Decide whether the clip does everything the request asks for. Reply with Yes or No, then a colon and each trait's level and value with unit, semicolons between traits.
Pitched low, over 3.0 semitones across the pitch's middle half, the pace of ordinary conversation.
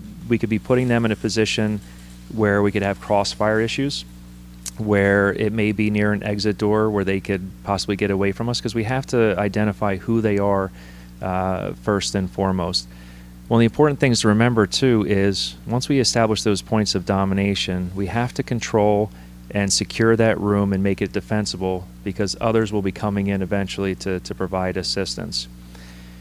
No: low, 100 Hz; average, 2.7 semitones; average, 190 wpm